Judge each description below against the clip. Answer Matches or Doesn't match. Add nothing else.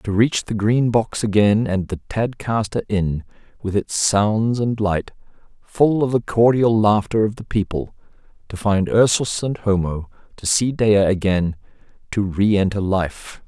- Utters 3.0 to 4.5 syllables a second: Matches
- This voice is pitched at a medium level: Doesn't match